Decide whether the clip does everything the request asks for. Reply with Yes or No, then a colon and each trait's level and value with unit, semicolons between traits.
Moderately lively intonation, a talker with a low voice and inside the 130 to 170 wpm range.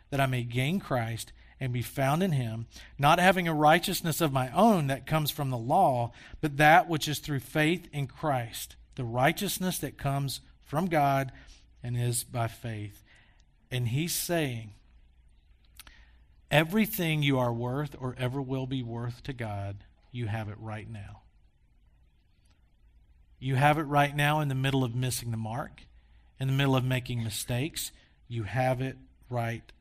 Yes: average, 4.4 semitones; low, 130 Hz; average, 165 wpm